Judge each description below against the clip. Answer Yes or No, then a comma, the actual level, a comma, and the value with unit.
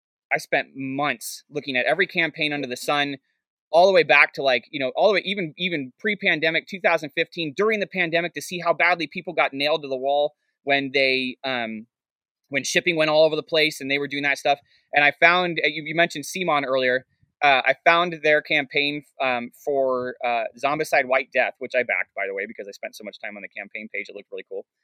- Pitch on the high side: No, medium, 150 Hz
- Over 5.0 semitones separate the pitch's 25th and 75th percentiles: No, average, 3.9 semitones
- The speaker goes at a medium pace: No, fast, 225 wpm